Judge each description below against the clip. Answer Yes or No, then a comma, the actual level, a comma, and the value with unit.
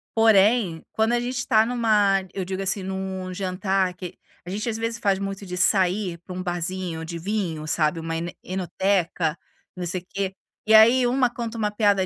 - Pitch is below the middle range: No, high, 190 Hz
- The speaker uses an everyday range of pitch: Yes, average, 3.3 semitones